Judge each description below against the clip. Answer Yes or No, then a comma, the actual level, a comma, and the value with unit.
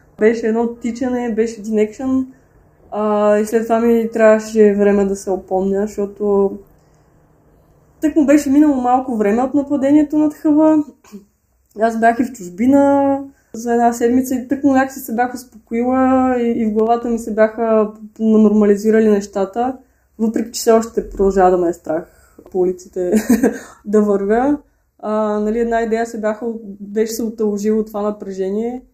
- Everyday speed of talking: Yes, average, 150 wpm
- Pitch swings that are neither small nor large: Yes, average, 3.1 semitones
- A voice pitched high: Yes, high, 225 Hz